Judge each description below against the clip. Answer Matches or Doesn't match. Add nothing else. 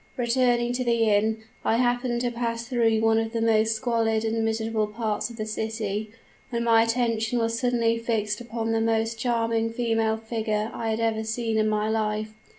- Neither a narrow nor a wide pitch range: Doesn't match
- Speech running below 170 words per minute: Doesn't match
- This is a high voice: Matches